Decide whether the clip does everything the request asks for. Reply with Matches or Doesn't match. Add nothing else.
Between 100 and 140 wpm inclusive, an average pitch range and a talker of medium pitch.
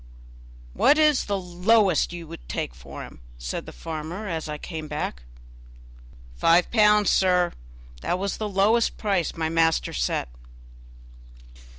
Matches